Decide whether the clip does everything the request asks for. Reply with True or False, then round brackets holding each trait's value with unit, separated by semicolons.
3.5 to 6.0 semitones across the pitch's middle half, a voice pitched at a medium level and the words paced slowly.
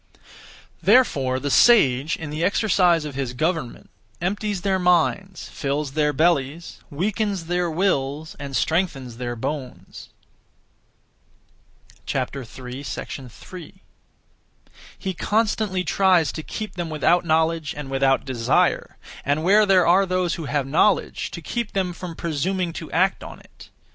True (5.1 semitones; 165 Hz; 130 wpm)